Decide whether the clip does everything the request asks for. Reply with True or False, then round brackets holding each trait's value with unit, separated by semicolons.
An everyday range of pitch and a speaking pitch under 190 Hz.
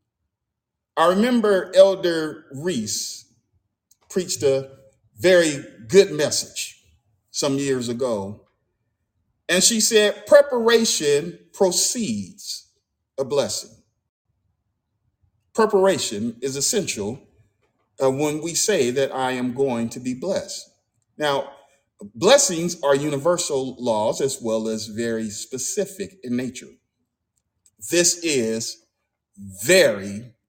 False (7.9 semitones; 140 Hz)